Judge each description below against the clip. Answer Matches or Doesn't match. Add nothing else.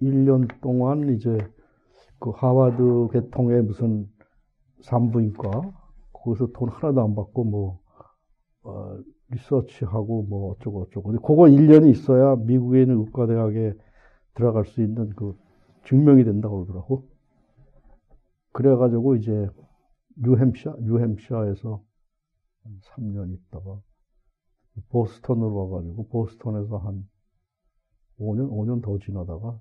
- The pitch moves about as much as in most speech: Matches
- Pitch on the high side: Doesn't match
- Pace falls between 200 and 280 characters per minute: Matches